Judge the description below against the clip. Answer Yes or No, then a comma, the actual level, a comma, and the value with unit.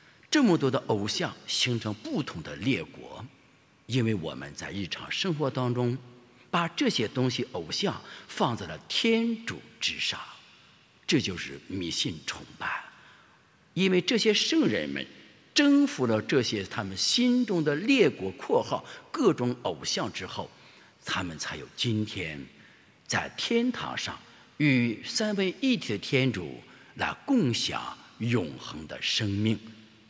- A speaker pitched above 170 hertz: No, low, 130 Hz